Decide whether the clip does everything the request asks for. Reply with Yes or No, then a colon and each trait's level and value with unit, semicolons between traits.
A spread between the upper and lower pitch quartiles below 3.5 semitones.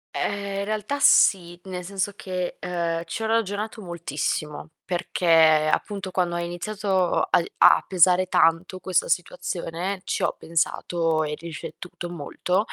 Yes: narrow, 2.6 semitones